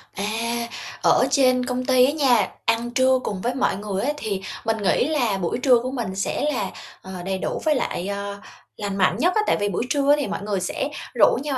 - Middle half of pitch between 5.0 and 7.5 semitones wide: No, average, 4.6 semitones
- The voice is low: No, high, 235 Hz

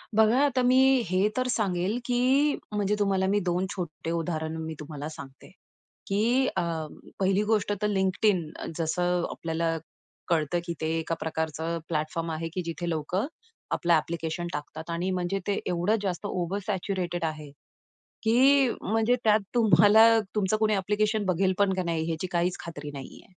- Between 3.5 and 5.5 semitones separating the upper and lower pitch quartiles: Yes, average, 4.1 semitones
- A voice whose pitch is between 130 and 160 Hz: No, medium, 185 Hz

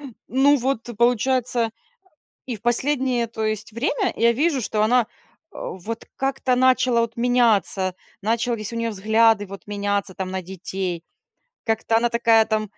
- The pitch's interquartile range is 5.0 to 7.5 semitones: No, average, 2.8 semitones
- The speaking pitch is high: Yes, high, 230 Hz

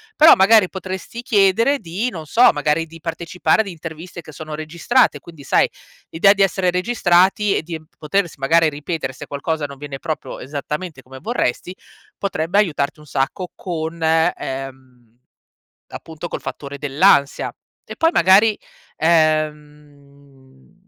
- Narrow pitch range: No, average, 4.4 semitones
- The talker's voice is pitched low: No, medium, 160 Hz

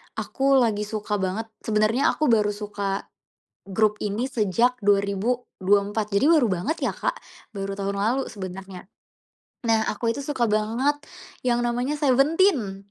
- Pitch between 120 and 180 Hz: No, high, 215 Hz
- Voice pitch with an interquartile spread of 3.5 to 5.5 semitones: Yes, average, 3.9 semitones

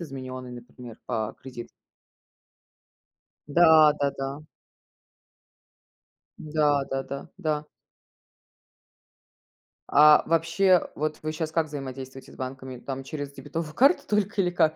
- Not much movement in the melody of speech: No, average, 3.2 semitones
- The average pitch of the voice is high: No, medium, 145 Hz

